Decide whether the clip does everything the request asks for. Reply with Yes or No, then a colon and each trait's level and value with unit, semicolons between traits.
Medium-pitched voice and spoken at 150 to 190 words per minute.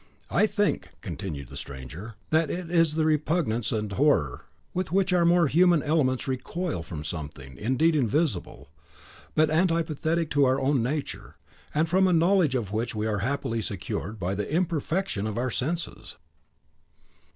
Yes: medium, 145 Hz; average, 155 wpm